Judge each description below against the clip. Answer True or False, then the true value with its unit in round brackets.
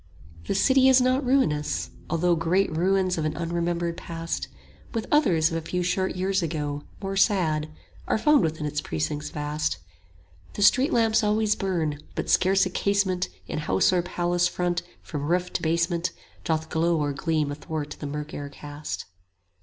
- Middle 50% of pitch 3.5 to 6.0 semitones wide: True (3.9 semitones)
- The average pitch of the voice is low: False (170 Hz)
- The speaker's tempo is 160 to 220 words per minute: True (175 wpm)